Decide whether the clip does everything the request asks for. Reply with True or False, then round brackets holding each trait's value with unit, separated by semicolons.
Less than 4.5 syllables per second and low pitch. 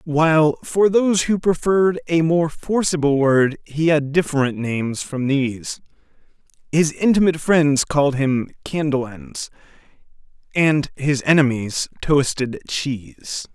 False (4.2 syllables/s; 150 Hz)